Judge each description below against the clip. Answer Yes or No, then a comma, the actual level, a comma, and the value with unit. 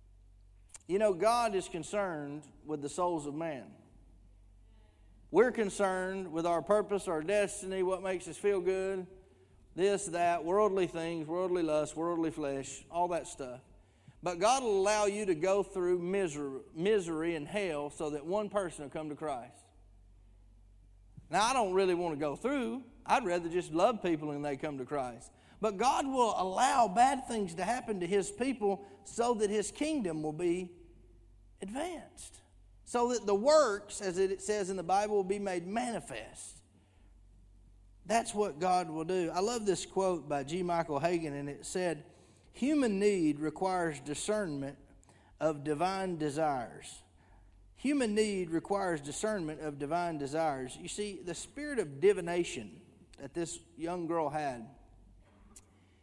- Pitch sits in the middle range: Yes, medium, 170 Hz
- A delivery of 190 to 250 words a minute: No, average, 155 wpm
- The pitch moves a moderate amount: No, wide, 6.3 semitones